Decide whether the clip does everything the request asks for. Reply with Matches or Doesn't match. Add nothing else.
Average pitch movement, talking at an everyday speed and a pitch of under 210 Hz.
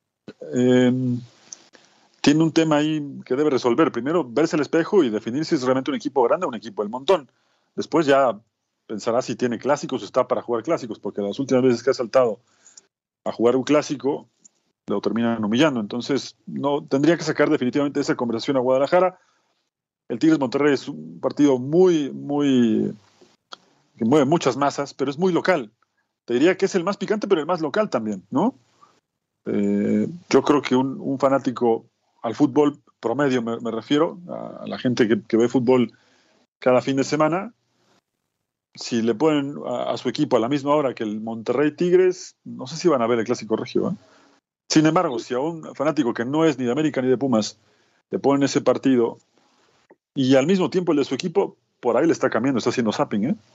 Doesn't match